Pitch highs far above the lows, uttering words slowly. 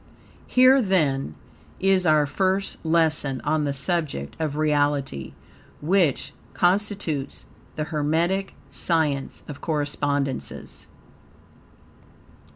No: average, 4.1 semitones; slow, 85 wpm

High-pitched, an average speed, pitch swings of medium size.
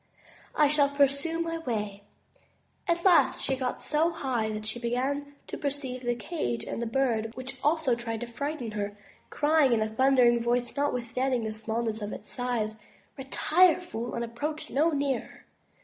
Yes: very high, 255 Hz; average, 165 wpm; average, 3.9 semitones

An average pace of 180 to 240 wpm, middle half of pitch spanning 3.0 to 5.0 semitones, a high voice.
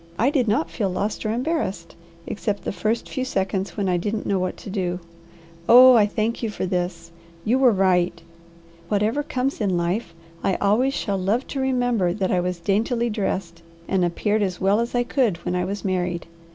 Yes: average, 195 wpm; average, 4.4 semitones; high, 200 Hz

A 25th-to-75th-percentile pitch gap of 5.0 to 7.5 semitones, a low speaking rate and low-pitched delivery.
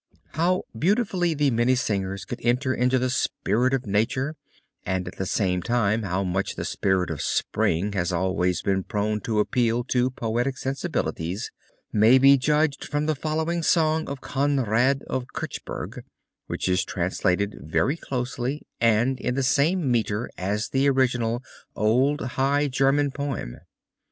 No: average, 5.3 semitones; average, 145 wpm; low, 125 Hz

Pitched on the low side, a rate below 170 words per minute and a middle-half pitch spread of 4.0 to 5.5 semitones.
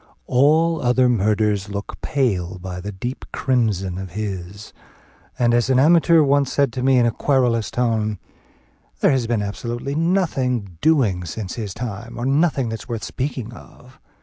Yes: low, 120 Hz; average, 160 wpm; average, 4.5 semitones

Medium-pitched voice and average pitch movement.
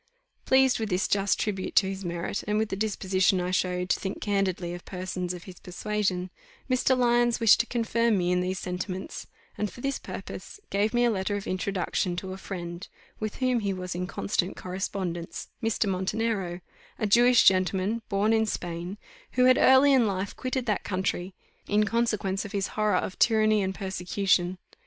No: high, 195 Hz; average, 3.2 semitones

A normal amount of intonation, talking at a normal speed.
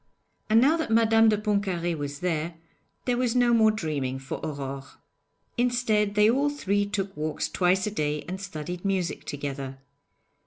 No: wide, 6.5 semitones; average, 160 wpm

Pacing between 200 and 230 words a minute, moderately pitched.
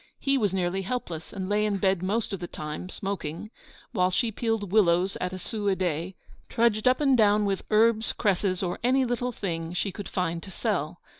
No: fast, 205 wpm; high, 195 Hz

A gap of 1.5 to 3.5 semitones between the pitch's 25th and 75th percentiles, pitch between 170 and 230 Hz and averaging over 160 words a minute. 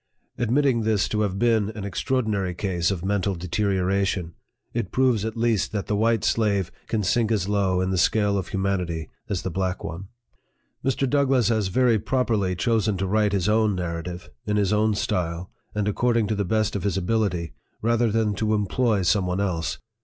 No: average, 3.1 semitones; low, 100 Hz; average, 190 wpm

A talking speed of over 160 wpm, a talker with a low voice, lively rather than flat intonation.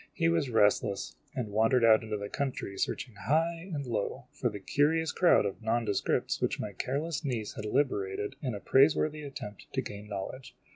Yes: average, 180 wpm; low, 120 Hz; wide, 5.7 semitones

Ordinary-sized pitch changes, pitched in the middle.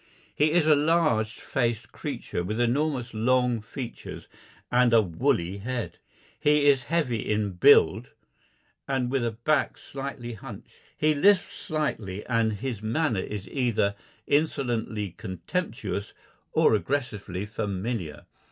No: average, 5.0 semitones; low, 120 Hz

